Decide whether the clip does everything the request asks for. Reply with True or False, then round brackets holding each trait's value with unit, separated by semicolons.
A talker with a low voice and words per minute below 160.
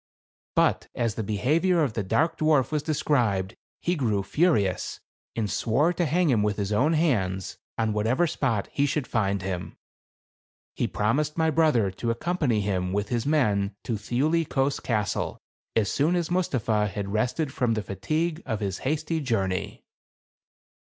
False (120 Hz; 165 wpm)